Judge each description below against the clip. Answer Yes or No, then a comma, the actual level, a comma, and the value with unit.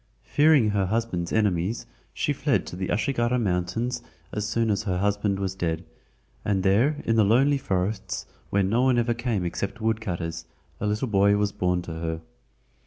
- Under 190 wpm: Yes, average, 175 wpm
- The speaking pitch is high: No, low, 105 Hz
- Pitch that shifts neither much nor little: Yes, average, 4.0 semitones